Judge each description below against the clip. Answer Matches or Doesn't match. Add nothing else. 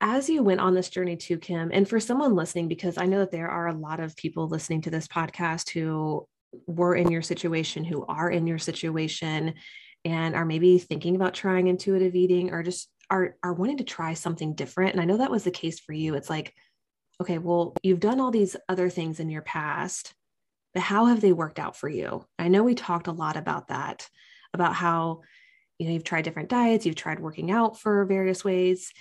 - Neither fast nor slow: Doesn't match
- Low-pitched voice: Doesn't match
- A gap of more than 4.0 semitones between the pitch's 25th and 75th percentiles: Doesn't match